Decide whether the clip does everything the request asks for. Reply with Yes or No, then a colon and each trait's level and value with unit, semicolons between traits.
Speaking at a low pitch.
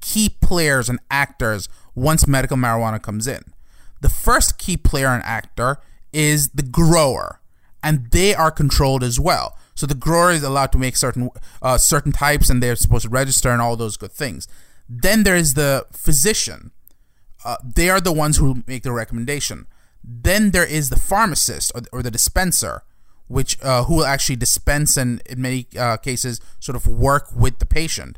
Yes: low, 130 Hz